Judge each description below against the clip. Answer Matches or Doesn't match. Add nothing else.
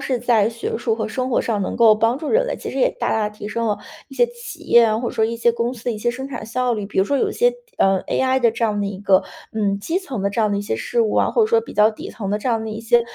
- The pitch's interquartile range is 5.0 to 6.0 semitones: Doesn't match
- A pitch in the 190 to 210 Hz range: Doesn't match